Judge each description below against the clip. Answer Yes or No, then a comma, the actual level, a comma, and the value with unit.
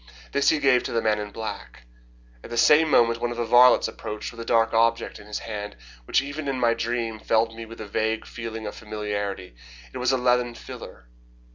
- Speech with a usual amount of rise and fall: No, narrow, 2.0 semitones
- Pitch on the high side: No, low, 115 Hz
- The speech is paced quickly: Yes, fast, 220 wpm